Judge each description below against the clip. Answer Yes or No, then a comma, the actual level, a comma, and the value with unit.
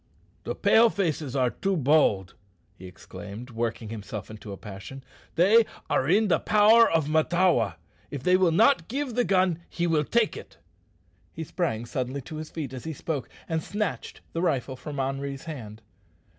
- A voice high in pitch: No, medium, 150 Hz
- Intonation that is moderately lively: No, wide, 6.8 semitones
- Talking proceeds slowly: No, average, 170 wpm